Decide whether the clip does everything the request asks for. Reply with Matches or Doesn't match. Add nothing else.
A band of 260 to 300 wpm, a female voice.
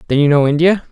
Doesn't match